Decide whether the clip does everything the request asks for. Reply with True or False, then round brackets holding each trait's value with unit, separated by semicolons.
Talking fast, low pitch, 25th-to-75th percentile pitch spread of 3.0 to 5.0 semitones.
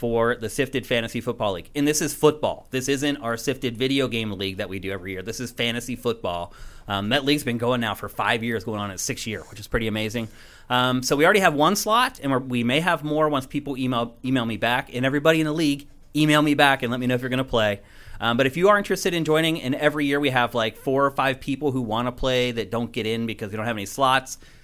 True (275 wpm; 125 Hz; 3.7 semitones)